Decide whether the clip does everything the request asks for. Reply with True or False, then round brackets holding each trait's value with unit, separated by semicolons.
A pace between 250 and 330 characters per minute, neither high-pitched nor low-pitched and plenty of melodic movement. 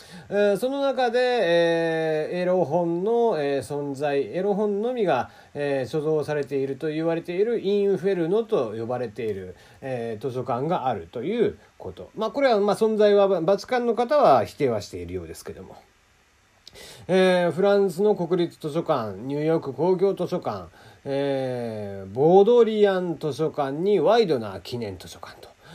True (295 characters per minute; 170 Hz; 6.4 semitones)